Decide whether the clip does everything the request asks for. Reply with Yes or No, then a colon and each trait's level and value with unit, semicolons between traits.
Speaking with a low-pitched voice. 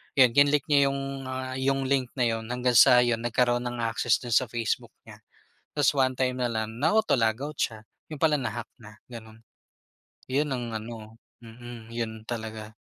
Yes: low, 120 Hz